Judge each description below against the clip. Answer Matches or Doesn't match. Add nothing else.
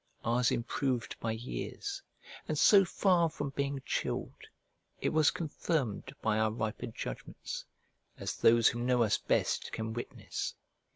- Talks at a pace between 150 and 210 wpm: Doesn't match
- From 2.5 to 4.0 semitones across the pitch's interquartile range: Doesn't match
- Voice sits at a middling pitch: Doesn't match